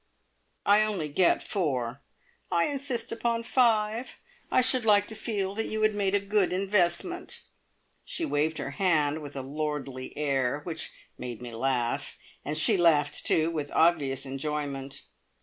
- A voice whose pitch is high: No, medium, 165 Hz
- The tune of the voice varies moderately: No, wide, 6.8 semitones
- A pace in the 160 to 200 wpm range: No, average, 150 wpm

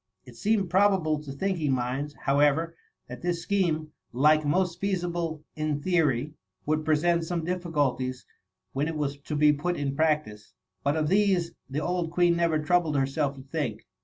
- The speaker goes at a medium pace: Yes, average, 165 wpm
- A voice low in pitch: No, medium, 155 Hz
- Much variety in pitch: No, average, 3.3 semitones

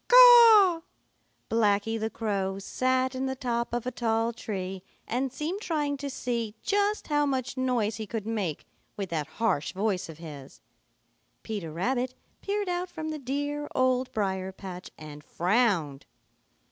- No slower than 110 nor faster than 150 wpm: Yes, average, 145 wpm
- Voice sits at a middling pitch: No, high, 230 Hz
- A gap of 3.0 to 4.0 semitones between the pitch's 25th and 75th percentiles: No, wide, 5.4 semitones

